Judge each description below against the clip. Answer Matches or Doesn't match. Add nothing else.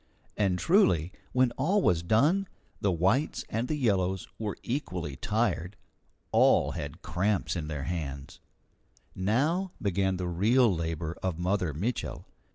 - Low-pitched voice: Matches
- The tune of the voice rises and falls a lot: Matches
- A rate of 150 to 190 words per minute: Doesn't match